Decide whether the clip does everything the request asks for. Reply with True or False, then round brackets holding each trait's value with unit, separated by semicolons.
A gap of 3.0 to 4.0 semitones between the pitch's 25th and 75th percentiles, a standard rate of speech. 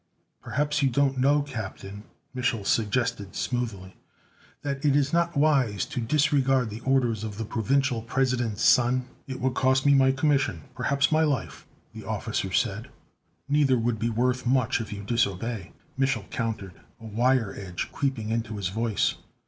True (3.6 semitones; 155 wpm)